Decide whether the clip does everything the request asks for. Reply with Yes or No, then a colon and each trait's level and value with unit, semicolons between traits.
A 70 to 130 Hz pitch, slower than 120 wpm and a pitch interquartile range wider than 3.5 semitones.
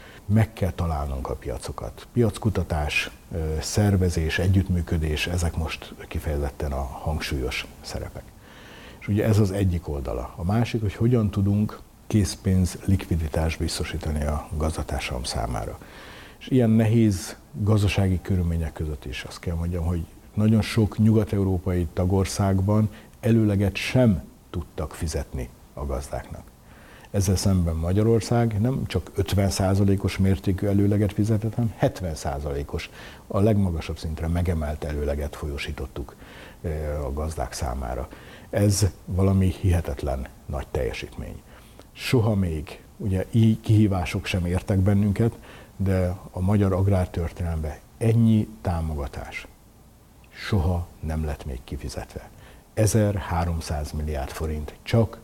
Yes: very low, 95 Hz; average, 110 wpm; average, 5.0 semitones